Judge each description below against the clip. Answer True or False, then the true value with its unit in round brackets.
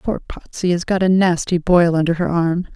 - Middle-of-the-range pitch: True (175 Hz)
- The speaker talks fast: True (220 wpm)